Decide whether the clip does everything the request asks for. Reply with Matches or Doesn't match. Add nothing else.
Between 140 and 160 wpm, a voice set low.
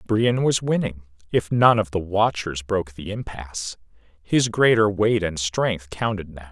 Matches